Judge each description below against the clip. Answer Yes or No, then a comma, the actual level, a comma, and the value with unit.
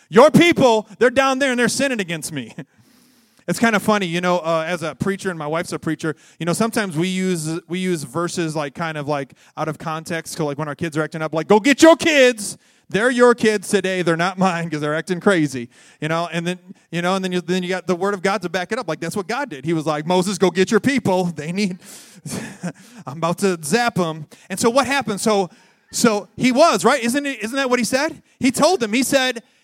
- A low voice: No, medium, 185 Hz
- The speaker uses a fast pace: Yes, fast, 255 wpm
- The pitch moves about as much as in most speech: No, wide, 5.8 semitones